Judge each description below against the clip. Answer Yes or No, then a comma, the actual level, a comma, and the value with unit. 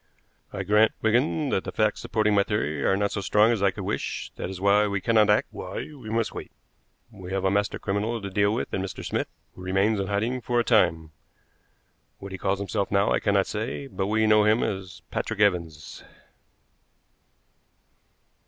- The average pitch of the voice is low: Yes, low, 100 Hz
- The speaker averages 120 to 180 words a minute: No, average, 195 wpm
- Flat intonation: Yes, narrow, 2.2 semitones